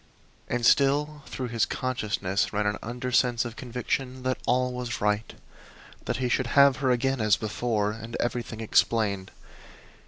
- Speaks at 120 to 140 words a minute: No, average, 150 wpm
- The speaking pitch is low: Yes, low, 120 Hz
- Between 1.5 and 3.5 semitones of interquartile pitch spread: Yes, average, 2.8 semitones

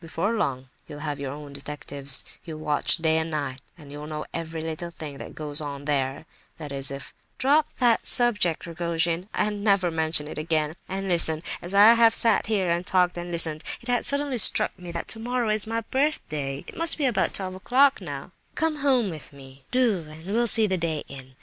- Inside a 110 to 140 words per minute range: No, average, 200 wpm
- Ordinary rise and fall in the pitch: No, wide, 6.4 semitones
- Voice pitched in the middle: Yes, medium, 170 Hz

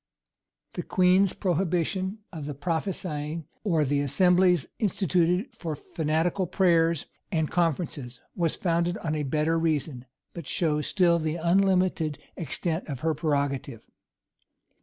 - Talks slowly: Yes, slow, 120 wpm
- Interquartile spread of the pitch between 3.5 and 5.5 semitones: No, average, 3.0 semitones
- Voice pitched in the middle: Yes, medium, 165 Hz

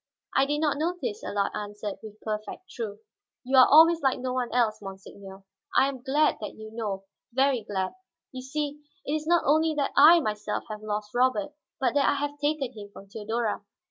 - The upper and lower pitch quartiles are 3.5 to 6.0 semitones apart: Yes, wide, 5.6 semitones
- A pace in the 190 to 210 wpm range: Yes, average, 195 wpm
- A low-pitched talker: No, very high, 250 Hz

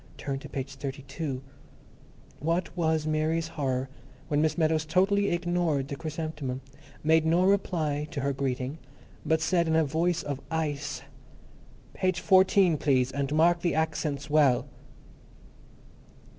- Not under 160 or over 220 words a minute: No, slow, 135 wpm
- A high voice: No, medium, 155 Hz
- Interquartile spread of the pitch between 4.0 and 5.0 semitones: No, average, 3.1 semitones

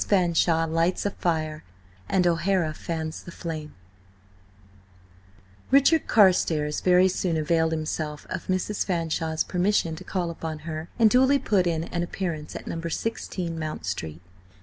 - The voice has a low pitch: No, medium, 170 Hz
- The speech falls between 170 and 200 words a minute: No, average, 140 wpm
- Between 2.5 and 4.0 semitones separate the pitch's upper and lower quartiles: Yes, average, 2.8 semitones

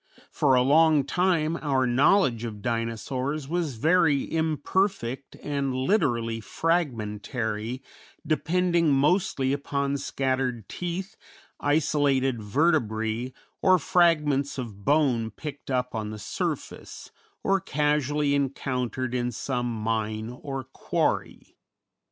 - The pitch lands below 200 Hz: Yes, low, 135 Hz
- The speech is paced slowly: Yes, slow, 105 wpm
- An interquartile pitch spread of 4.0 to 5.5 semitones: Yes, average, 4.4 semitones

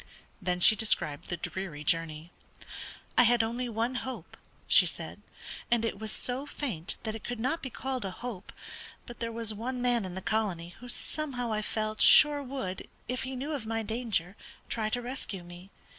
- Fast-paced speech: No, average, 190 wpm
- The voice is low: No, high, 225 Hz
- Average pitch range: Yes, average, 4.6 semitones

